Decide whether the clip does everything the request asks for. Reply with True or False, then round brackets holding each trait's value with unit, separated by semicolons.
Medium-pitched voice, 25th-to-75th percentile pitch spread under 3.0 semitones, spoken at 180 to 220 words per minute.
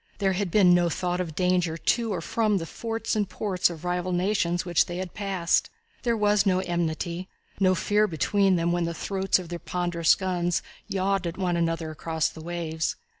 True (180 Hz; 2.4 semitones; 200 wpm)